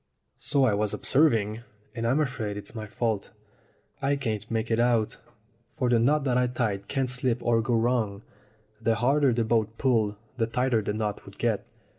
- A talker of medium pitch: No, low, 115 Hz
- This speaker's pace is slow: No, average, 185 wpm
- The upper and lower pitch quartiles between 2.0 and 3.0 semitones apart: Yes, average, 2.7 semitones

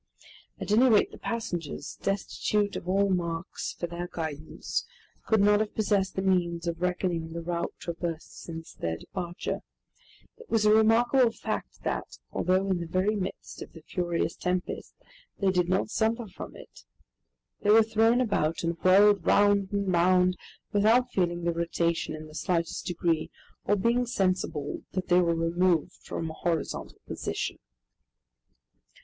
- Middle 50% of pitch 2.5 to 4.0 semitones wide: Yes, average, 3.5 semitones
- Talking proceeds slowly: No, average, 155 wpm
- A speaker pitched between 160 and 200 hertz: Yes, medium, 185 Hz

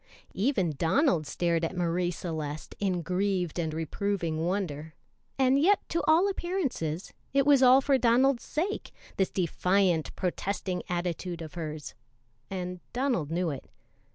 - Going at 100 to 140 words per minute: Yes, slow, 135 wpm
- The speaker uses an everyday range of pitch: No, wide, 7.5 semitones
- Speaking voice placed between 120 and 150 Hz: No, medium, 180 Hz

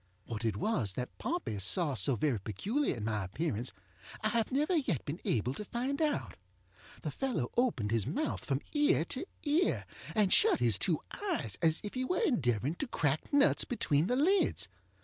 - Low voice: No, medium, 165 Hz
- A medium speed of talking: Yes, average, 185 wpm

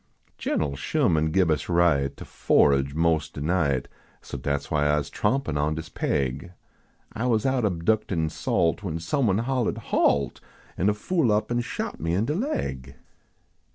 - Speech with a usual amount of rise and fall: No, wide, 6.8 semitones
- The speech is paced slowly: No, average, 175 wpm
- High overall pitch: No, very low, 85 Hz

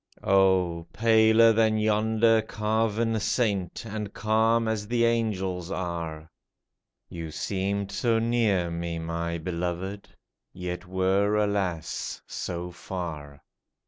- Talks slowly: Yes, slow, 105 wpm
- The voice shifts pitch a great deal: No, average, 4.1 semitones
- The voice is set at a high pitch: No, low, 100 Hz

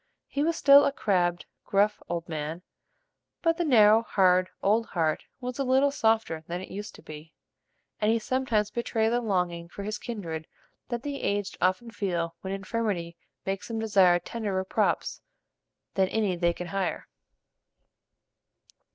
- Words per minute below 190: Yes, average, 155 wpm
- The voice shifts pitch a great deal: No, average, 4.6 semitones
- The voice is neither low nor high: No, high, 200 Hz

